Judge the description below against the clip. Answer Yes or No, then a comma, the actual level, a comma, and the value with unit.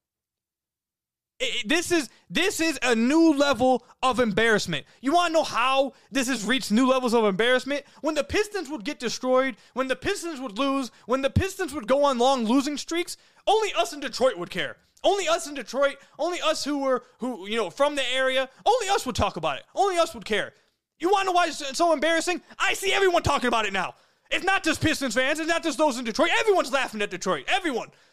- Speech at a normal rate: No, fast, 220 wpm